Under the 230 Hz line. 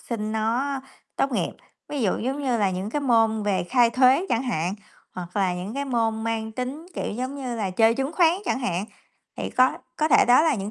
No: high, 235 Hz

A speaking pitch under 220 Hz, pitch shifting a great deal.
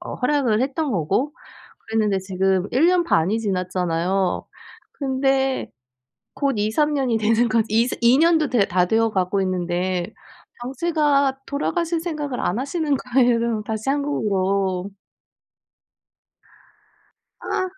No: high, 235 Hz; wide, 6.5 semitones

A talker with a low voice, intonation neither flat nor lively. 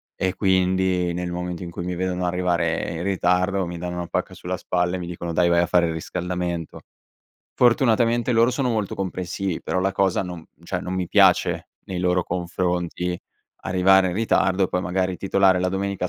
No: very low, 90 Hz; narrow, 1.5 semitones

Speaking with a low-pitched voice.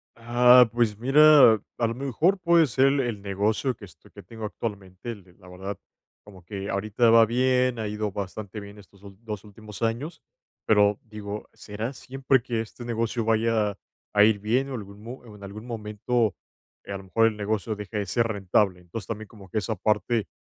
Yes: low, 110 Hz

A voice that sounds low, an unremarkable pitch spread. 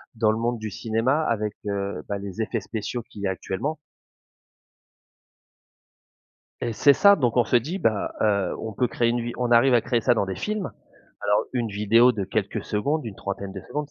Yes: low, 115 Hz; average, 3.2 semitones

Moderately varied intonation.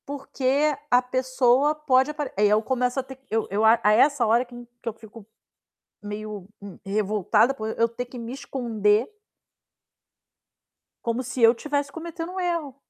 Yes: average, 3.9 semitones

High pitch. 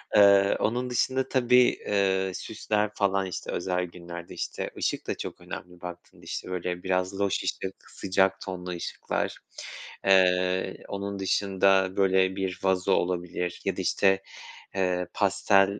No: very low, 95 Hz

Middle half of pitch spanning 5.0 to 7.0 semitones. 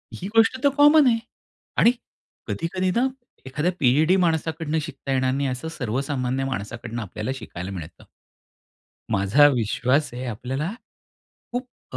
Yes: wide, 5.5 semitones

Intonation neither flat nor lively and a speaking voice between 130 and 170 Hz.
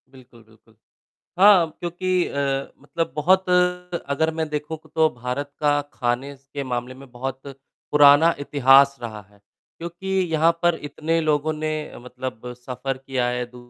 Yes: average, 4.1 semitones; medium, 140 Hz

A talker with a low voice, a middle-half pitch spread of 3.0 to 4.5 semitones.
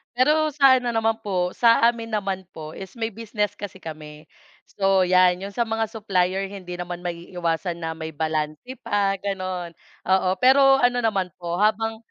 No: high, 195 Hz; average, 4.1 semitones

